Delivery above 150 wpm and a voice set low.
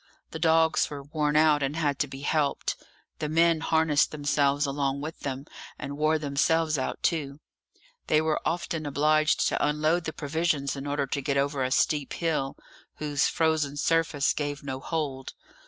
No: average, 170 wpm; medium, 150 Hz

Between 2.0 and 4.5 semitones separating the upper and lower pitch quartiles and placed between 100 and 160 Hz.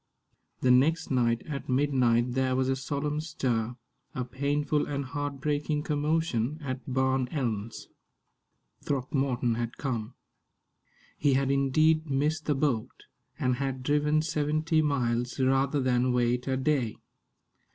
Yes: average, 2.8 semitones; low, 135 Hz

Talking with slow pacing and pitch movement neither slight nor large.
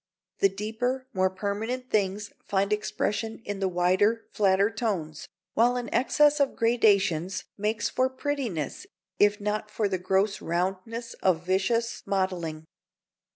Yes: slow, 130 wpm; average, 3.4 semitones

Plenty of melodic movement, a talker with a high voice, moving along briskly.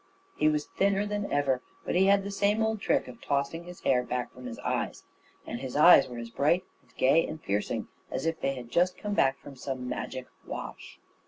No: wide, 7.1 semitones; medium, 145 Hz; fast, 220 wpm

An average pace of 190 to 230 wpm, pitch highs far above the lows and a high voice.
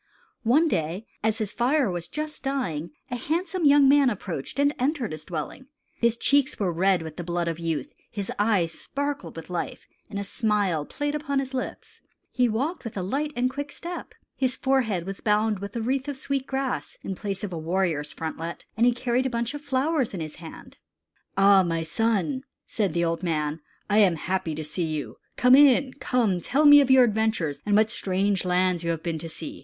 Yes: fast, 205 wpm; wide, 7.5 semitones; high, 215 Hz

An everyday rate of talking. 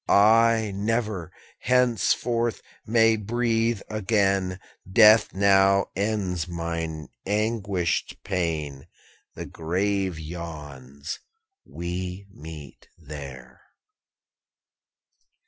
No: slow, 70 wpm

